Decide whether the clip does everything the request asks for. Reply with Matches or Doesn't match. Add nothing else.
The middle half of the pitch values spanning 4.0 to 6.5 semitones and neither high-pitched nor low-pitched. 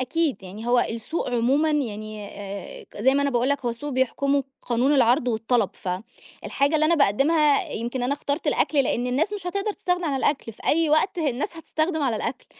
Doesn't match